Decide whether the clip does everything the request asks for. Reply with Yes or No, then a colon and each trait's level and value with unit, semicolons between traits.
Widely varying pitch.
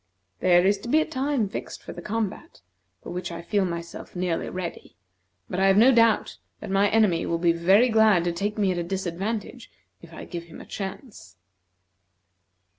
No: average, 3.9 semitones